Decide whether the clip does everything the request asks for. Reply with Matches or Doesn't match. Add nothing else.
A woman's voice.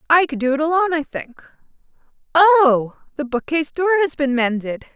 Matches